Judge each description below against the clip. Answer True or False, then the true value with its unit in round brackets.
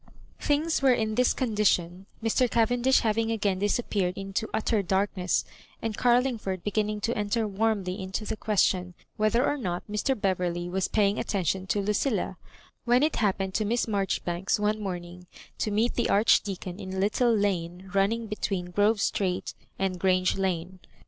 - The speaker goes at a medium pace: True (155 wpm)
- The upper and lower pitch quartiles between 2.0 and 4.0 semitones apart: True (3.1 semitones)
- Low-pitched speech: False (205 Hz)